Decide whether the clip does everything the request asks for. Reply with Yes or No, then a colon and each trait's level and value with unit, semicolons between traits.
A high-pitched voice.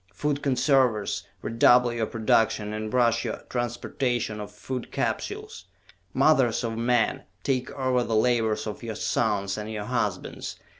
No: low, 115 Hz